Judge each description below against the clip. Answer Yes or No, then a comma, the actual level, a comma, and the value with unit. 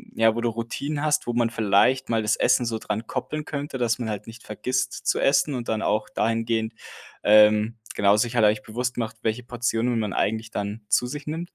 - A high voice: No, low, 115 Hz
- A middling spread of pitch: No, narrow, 2.2 semitones